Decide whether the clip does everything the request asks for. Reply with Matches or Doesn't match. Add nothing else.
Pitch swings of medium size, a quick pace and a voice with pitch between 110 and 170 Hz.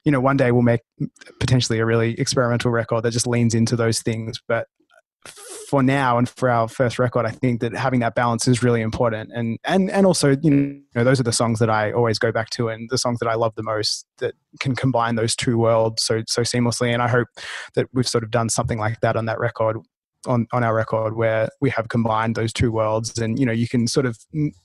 Doesn't match